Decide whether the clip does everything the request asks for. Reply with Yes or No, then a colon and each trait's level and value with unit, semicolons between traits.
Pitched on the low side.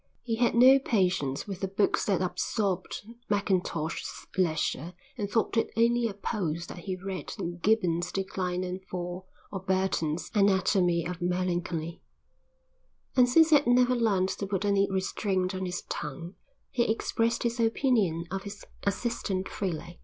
No: high, 190 Hz